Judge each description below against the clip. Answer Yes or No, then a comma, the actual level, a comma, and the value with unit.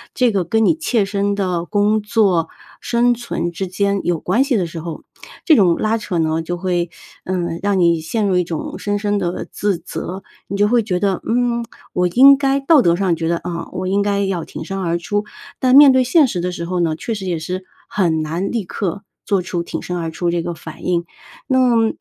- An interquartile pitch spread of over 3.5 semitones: Yes, average, 3.9 semitones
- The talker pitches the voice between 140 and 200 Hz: Yes, high, 190 Hz